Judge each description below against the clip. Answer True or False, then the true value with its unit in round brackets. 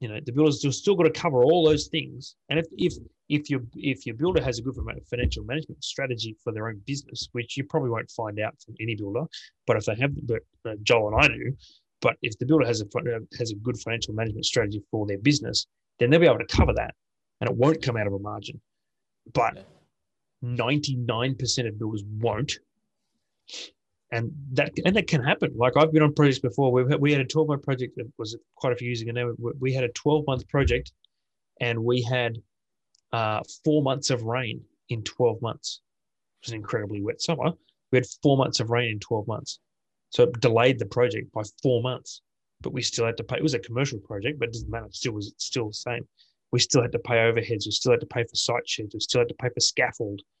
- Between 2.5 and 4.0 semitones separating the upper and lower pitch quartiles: True (3.7 semitones)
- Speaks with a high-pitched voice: False (125 Hz)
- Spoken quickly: True (230 wpm)